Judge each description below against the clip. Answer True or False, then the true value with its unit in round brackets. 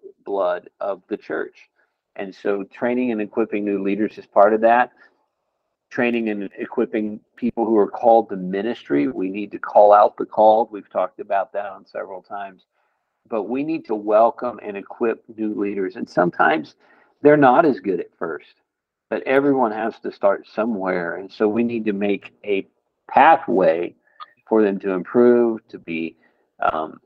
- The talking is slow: False (170 wpm)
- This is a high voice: False (110 Hz)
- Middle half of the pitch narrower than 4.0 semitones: True (3.1 semitones)